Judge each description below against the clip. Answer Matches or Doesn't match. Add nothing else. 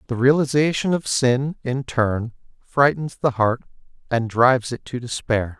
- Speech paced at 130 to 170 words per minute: Matches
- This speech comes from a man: Matches